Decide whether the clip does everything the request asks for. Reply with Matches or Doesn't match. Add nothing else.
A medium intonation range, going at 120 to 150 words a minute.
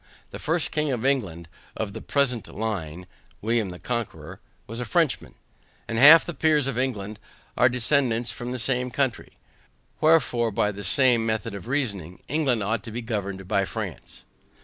Doesn't match